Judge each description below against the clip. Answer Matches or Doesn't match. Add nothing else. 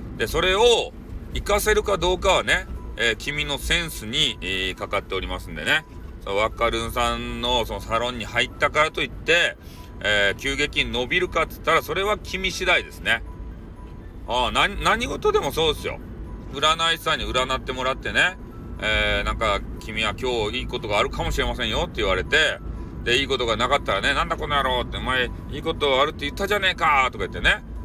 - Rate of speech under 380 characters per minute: Doesn't match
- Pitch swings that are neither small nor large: Doesn't match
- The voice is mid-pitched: Doesn't match